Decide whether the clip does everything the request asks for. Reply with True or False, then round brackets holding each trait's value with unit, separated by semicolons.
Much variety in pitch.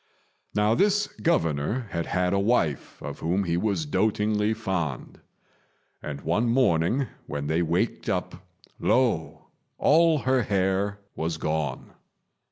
True (6.5 semitones)